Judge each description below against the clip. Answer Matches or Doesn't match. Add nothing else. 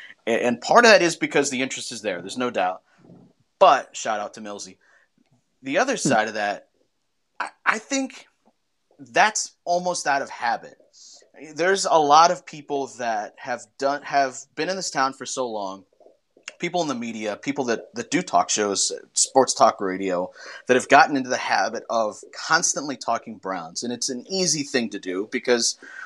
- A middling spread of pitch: Doesn't match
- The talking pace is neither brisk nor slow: Matches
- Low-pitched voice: Matches